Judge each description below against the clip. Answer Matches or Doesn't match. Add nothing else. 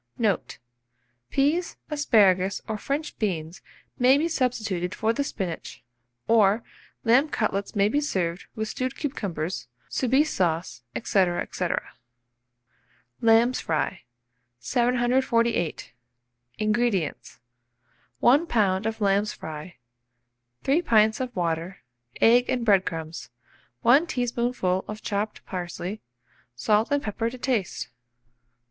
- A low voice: Doesn't match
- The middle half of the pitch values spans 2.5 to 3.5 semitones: Doesn't match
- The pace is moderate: Doesn't match